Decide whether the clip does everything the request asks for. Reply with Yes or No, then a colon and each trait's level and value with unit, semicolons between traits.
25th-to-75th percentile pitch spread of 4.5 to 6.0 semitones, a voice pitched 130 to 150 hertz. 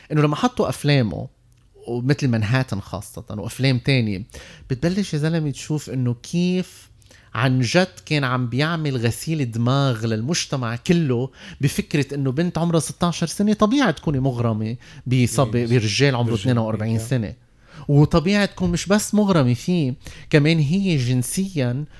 Yes: wide, 5.4 semitones; low, 135 Hz